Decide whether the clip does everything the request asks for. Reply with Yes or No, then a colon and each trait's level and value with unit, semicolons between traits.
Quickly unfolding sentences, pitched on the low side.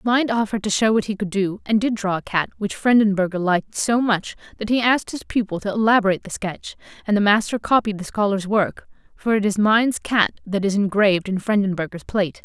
No: fast, 215 wpm; high, 205 Hz